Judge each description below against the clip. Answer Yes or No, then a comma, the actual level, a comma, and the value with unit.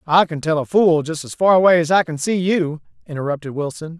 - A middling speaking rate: No, fast, 240 wpm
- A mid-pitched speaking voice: Yes, medium, 165 Hz